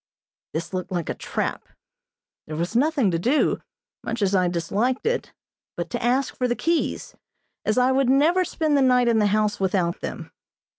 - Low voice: No, high, 235 Hz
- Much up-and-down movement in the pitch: Yes, wide, 6.5 semitones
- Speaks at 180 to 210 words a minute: Yes, average, 185 wpm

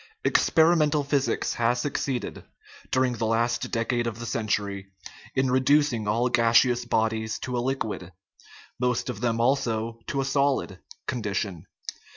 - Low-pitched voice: Yes, low, 120 Hz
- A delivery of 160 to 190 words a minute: No, average, 140 wpm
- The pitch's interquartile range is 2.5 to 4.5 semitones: Yes, average, 2.8 semitones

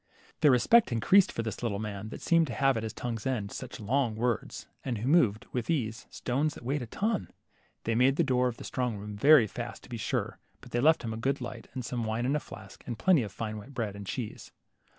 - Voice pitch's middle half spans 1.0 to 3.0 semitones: No, average, 3.7 semitones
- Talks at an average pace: No, fast, 265 wpm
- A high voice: No, low, 120 Hz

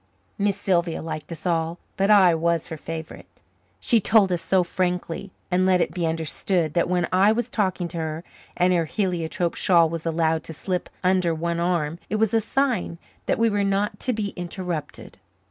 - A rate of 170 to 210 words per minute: Yes, average, 190 wpm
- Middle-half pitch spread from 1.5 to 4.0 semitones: Yes, average, 2.9 semitones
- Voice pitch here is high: No, medium, 180 Hz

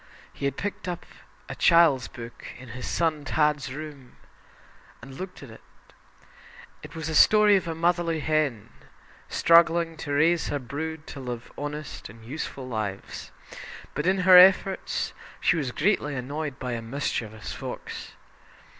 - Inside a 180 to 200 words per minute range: No, average, 150 wpm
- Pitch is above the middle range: No, medium, 150 Hz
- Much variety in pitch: No, average, 4.6 semitones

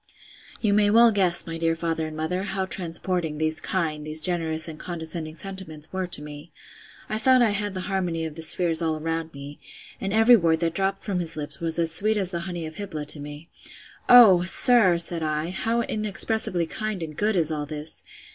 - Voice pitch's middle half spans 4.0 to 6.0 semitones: No, average, 3.5 semitones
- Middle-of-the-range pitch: Yes, medium, 170 Hz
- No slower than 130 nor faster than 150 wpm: No, average, 200 wpm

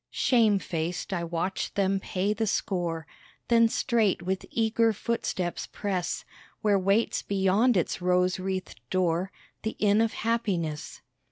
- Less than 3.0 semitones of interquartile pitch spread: No, average, 3.4 semitones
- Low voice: No, high, 195 Hz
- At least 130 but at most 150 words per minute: Yes, slow, 135 wpm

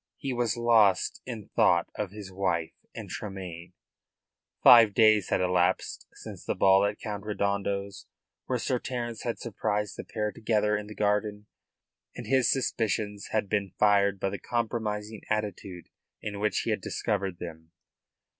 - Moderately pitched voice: No, low, 105 Hz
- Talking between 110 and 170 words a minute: Yes, average, 155 wpm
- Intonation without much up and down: Yes, narrow, 1.9 semitones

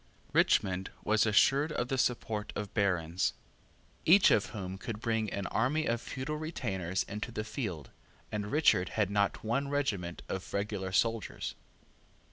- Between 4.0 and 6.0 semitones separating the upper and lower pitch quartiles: Yes, average, 4.4 semitones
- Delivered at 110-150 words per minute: Yes, average, 145 wpm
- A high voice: No, low, 105 Hz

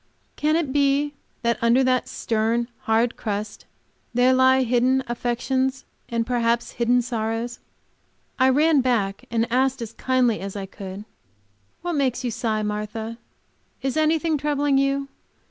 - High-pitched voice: Yes, high, 245 Hz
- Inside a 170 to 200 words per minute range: No, average, 145 wpm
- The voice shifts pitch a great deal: No, average, 2.8 semitones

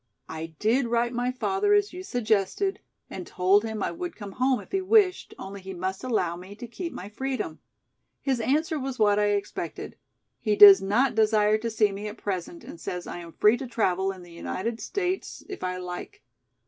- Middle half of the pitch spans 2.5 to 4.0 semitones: No, wide, 5.4 semitones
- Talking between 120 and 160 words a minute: No, average, 200 wpm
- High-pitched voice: Yes, high, 215 Hz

